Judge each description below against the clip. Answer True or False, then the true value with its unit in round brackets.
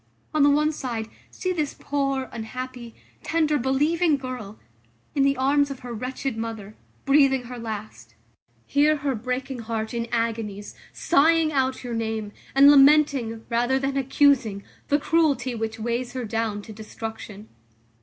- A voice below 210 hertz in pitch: False (255 Hz)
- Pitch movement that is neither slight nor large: True (3.9 semitones)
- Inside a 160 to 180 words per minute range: False (145 wpm)